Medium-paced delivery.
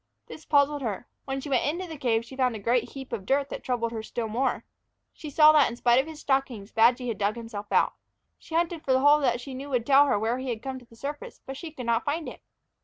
No: fast, 280 wpm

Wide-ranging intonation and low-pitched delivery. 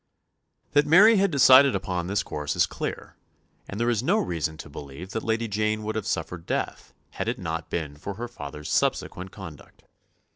Yes: wide, 6.6 semitones; low, 100 Hz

